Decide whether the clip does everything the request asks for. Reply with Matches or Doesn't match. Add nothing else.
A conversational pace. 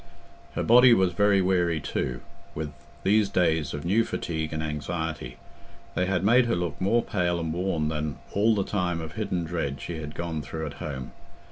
Matches